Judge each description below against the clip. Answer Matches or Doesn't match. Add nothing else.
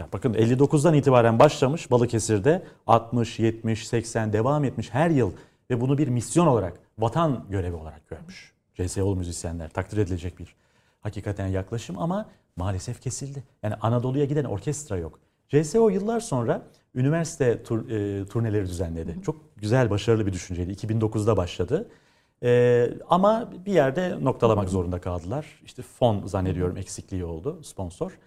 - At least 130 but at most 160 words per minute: Matches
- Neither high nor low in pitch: Doesn't match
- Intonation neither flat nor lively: Doesn't match